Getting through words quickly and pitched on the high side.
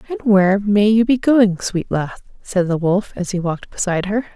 Yes: fast, 220 wpm; high, 200 Hz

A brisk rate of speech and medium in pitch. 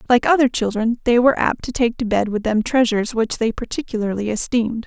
No: fast, 210 wpm; high, 230 Hz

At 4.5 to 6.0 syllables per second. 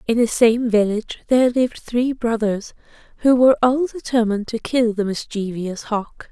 Yes: 5.1 syllables/s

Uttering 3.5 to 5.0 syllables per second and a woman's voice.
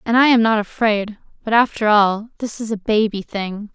Yes: 4.9 syllables/s; female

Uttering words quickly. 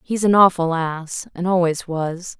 No: average, 150 wpm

